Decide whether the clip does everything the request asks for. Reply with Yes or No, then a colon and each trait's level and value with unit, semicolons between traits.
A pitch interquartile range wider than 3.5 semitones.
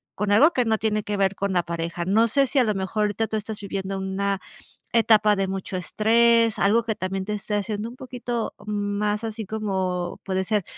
No: narrow, 2.4 semitones